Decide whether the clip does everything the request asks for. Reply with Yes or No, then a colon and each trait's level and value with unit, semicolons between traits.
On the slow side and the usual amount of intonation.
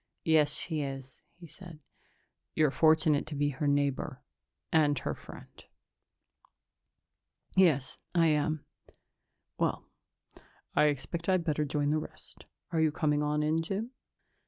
No: slow, 130 wpm; narrow, 1.9 semitones